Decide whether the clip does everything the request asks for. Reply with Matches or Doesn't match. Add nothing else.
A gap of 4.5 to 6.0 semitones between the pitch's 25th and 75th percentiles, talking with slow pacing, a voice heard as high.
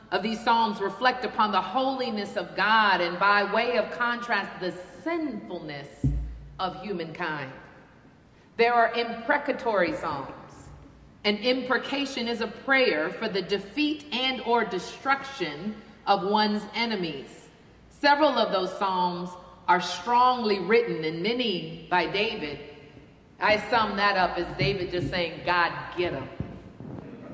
Matches